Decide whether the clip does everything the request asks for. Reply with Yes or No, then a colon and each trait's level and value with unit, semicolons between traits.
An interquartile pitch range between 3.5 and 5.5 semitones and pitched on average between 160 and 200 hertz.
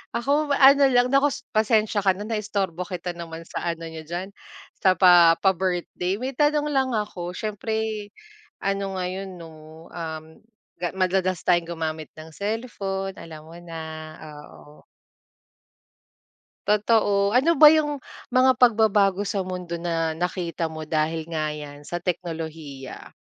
Yes: average, 4.6 semitones; medium, 185 Hz